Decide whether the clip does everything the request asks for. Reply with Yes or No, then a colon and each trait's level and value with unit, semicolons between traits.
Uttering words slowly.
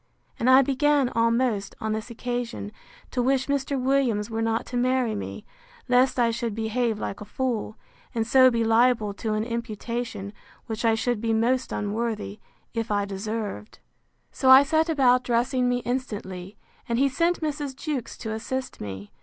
No: average, 170 wpm